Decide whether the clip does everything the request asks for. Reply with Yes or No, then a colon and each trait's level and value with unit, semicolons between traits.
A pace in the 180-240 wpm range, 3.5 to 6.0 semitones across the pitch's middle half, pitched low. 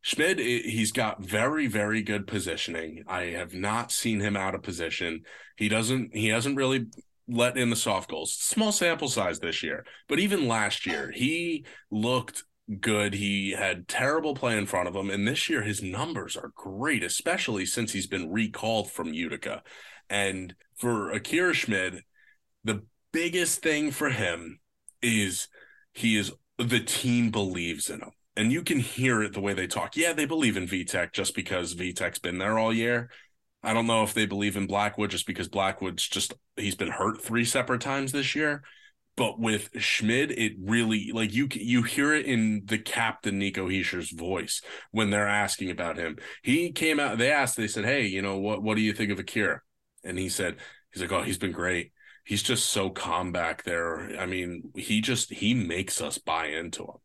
Yes: average, 190 wpm; average, 3.8 semitones; low, 105 Hz